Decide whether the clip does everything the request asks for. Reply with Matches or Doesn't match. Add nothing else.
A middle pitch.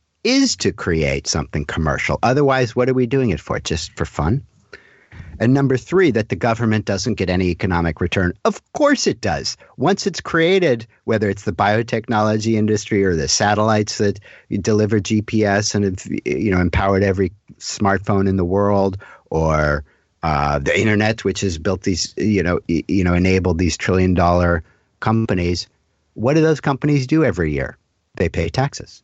Doesn't match